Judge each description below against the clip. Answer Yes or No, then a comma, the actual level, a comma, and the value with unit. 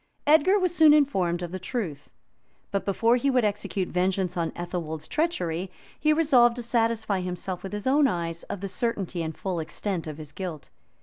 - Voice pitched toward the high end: Yes, high, 195 Hz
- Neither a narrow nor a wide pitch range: No, wide, 5.9 semitones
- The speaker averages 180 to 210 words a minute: Yes, average, 185 wpm